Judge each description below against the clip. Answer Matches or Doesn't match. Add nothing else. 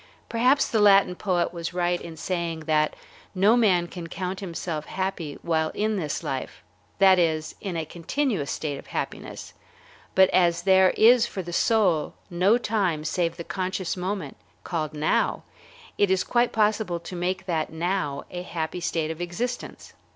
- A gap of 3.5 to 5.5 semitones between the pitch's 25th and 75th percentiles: Doesn't match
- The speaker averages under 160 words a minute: Doesn't match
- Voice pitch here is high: Doesn't match